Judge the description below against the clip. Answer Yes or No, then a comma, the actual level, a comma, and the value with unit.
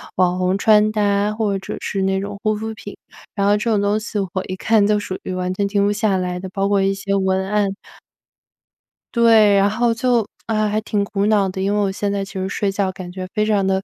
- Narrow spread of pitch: Yes, narrow, 1.6 semitones